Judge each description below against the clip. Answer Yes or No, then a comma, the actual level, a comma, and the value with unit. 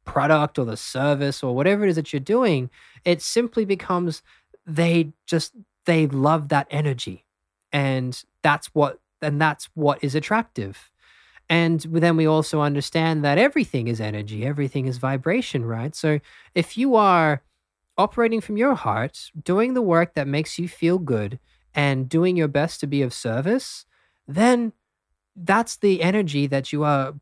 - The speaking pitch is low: No, medium, 155 Hz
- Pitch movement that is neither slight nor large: Yes, average, 4.1 semitones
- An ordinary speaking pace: Yes, average, 160 wpm